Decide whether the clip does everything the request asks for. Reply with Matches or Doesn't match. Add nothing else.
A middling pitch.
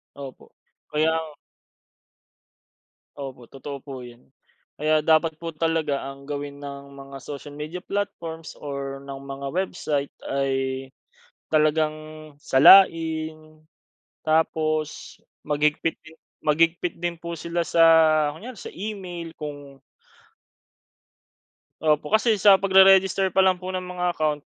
Matches